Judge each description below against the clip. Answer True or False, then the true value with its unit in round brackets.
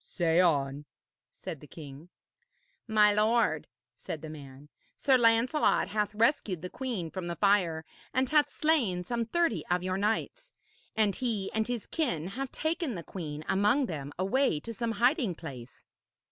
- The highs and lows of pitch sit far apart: True (6.8 semitones)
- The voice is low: False (205 Hz)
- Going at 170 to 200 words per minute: False (160 wpm)